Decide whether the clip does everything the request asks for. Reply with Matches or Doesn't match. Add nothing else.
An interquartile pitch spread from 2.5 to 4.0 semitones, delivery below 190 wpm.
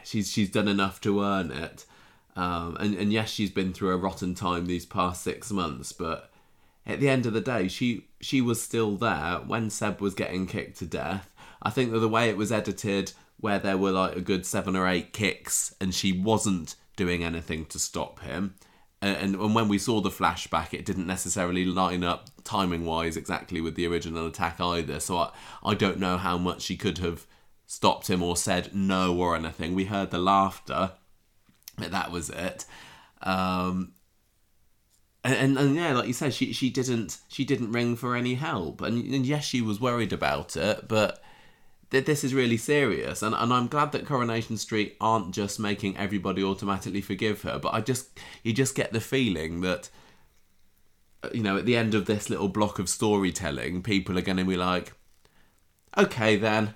Doesn't match